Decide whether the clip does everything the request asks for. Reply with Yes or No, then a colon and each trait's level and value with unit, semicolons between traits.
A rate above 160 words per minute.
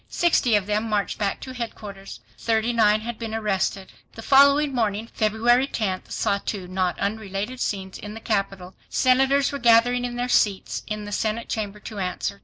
Yes: average, 180 wpm